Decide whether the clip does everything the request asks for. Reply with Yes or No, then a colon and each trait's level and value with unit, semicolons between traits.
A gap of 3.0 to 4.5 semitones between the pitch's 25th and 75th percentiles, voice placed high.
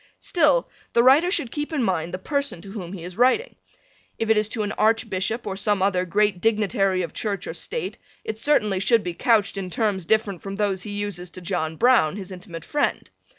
Yes: average, 3.7 semitones; high, 205 Hz